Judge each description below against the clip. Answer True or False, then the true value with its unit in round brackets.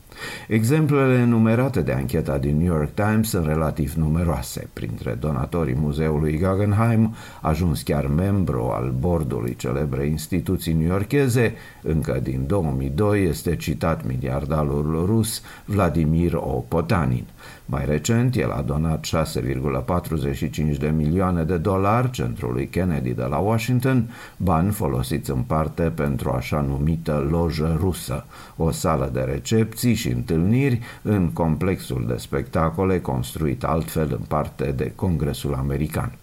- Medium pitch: False (80 Hz)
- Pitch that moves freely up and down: True (6.1 semitones)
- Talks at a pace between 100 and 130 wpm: True (125 wpm)